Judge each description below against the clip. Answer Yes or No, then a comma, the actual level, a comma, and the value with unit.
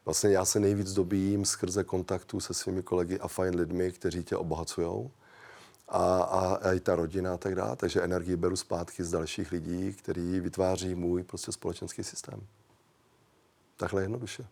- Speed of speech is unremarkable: Yes, average, 160 wpm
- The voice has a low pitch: Yes, very low, 95 Hz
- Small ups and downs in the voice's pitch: Yes, narrow, 1.7 semitones